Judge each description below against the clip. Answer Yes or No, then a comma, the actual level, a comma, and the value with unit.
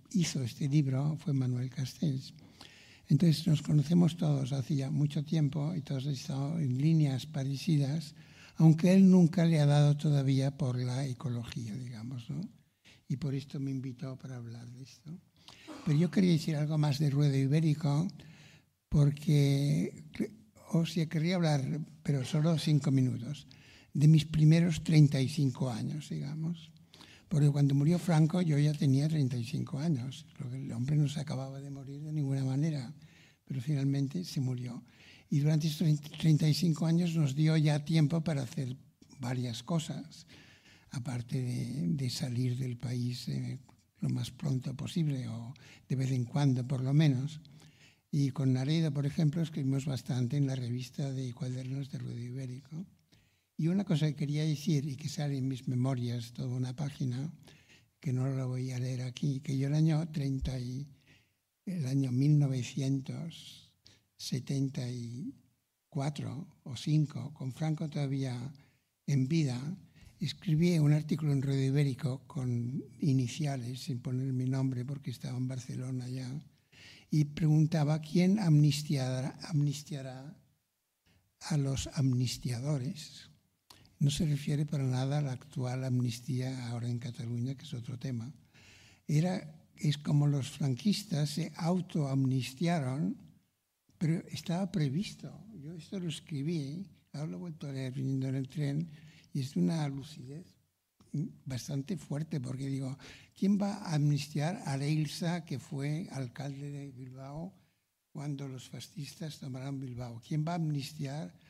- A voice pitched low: No, medium, 145 Hz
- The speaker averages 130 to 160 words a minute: Yes, average, 140 wpm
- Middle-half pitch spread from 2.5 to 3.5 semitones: Yes, average, 3.1 semitones